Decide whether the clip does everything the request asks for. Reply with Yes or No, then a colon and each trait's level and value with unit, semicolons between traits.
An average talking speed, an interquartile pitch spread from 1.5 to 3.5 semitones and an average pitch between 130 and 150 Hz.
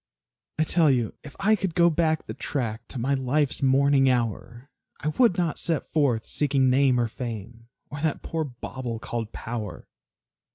No: average, 170 wpm; average, 4.3 semitones; low, 135 Hz